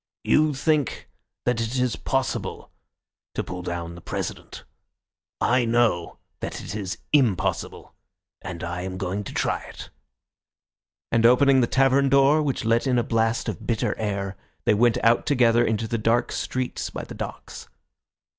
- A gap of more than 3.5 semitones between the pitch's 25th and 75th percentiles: Yes, average, 4.1 semitones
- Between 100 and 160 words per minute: Yes, average, 155 wpm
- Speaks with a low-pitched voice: Yes, low, 115 Hz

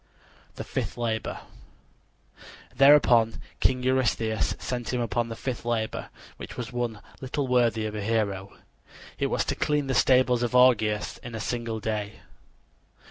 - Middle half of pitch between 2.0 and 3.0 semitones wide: Yes, narrow, 2.4 semitones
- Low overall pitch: Yes, low, 120 Hz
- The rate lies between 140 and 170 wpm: Yes, average, 145 wpm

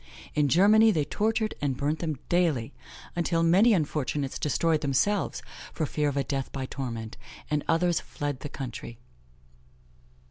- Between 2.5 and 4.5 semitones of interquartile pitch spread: Yes, average, 4.1 semitones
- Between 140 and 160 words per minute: Yes, average, 145 wpm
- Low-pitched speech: No, medium, 150 Hz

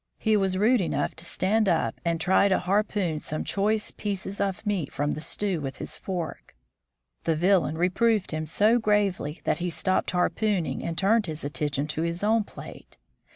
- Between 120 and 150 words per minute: No, average, 185 wpm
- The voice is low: No, medium, 185 Hz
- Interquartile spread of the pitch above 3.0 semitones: Yes, average, 4.3 semitones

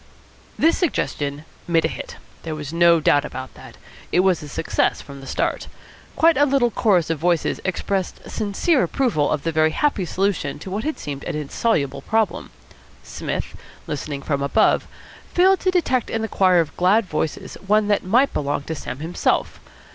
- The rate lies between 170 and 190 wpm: Yes, average, 180 wpm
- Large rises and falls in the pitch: Yes, wide, 6.8 semitones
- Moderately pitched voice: Yes, medium, 175 Hz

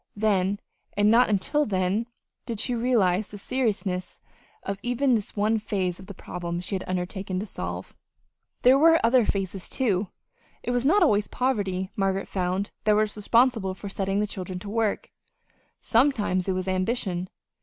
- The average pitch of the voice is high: Yes, high, 205 Hz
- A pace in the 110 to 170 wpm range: Yes, average, 165 wpm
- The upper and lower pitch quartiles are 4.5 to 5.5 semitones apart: No, average, 3.6 semitones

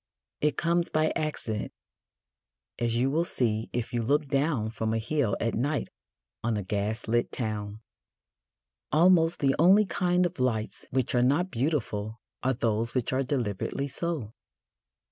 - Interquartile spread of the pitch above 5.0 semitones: Yes, wide, 5.6 semitones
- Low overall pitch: Yes, low, 125 Hz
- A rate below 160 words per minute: Yes, average, 150 wpm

